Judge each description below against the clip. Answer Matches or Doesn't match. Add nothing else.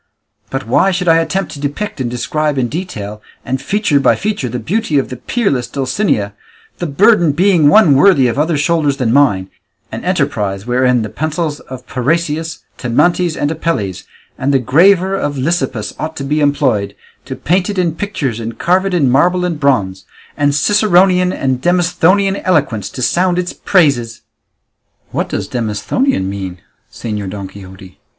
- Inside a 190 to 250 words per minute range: Doesn't match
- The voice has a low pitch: Doesn't match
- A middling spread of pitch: Doesn't match